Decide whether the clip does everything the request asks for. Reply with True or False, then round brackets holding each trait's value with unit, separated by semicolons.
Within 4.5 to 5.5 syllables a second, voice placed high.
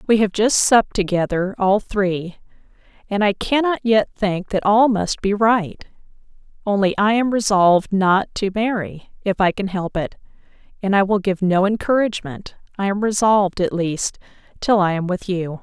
True (4.7 syllables/s; 200 Hz)